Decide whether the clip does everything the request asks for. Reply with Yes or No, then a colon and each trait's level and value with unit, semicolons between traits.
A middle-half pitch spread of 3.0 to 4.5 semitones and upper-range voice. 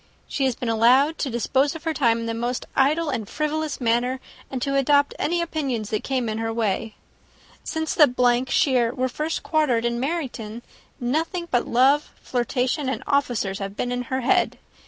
Yes: average, 3.8 semitones; very high, 255 Hz